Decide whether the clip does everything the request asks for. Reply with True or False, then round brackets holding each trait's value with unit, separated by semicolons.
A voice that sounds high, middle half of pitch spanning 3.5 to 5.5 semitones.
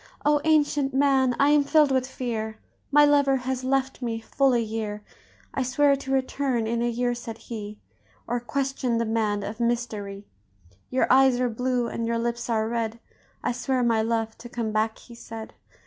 False (240 Hz; 2.9 semitones)